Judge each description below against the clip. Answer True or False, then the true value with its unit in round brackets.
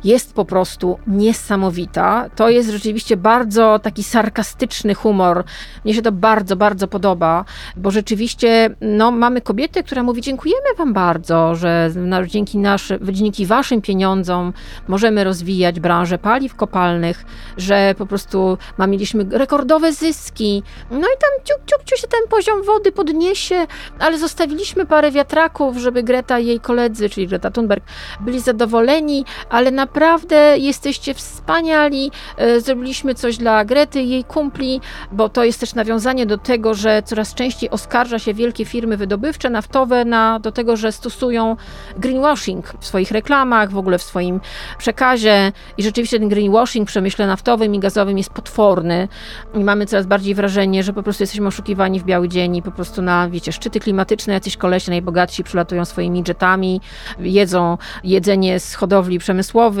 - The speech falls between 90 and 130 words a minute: False (155 wpm)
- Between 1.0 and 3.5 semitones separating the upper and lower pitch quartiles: False (4.5 semitones)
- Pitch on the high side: True (220 Hz)